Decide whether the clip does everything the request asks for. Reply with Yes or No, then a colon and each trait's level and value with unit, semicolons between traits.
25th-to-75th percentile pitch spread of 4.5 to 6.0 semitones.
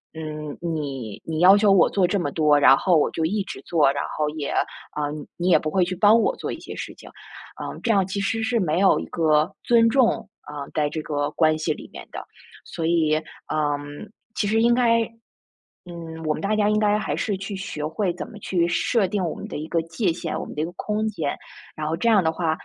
Yes: average, 5.0 semitones